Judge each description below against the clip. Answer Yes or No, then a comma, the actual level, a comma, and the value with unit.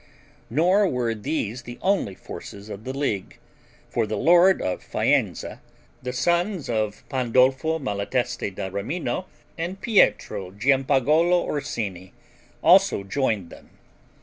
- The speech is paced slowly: Yes, slow, 120 wpm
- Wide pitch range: Yes, wide, 7.4 semitones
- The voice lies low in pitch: Yes, low, 125 Hz